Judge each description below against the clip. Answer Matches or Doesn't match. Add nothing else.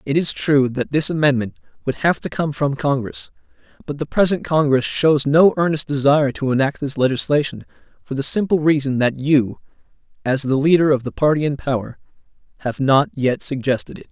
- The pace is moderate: Matches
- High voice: Doesn't match